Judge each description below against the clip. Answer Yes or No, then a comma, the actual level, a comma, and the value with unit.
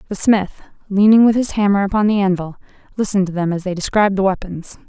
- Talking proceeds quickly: Yes, fast, 210 wpm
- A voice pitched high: Yes, high, 195 Hz